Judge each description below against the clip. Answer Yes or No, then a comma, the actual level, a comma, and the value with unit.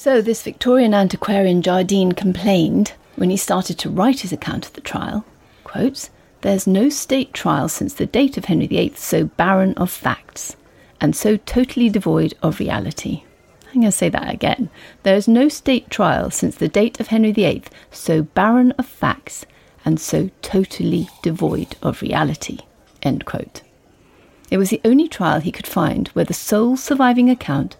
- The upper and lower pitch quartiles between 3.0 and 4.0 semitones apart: No, average, 4.8 semitones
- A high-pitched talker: Yes, high, 210 Hz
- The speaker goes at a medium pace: Yes, average, 170 wpm